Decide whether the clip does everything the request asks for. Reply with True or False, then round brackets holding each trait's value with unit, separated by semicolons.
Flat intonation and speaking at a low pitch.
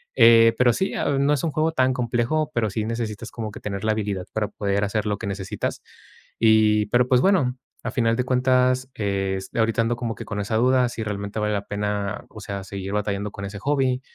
False (3.7 semitones; 110 Hz)